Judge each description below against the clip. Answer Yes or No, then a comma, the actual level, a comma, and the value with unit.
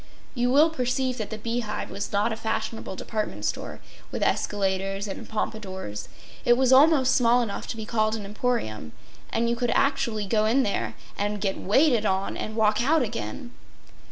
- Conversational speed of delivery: Yes, average, 180 wpm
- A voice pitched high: Yes, high, 220 Hz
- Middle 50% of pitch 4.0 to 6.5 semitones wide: No, average, 3.5 semitones